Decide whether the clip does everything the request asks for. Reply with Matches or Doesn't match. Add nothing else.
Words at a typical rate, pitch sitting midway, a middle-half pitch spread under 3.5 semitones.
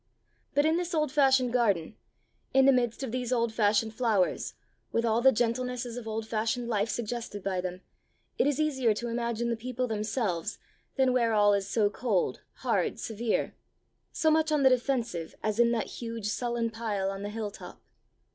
Doesn't match